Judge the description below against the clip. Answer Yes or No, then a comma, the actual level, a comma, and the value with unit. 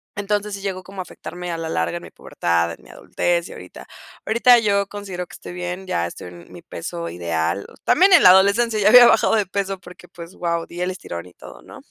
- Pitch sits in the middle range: Yes, medium, 180 Hz